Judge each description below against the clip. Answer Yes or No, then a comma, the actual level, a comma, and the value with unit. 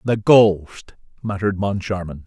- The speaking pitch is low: Yes, low, 100 Hz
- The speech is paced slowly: Yes, slow, 105 wpm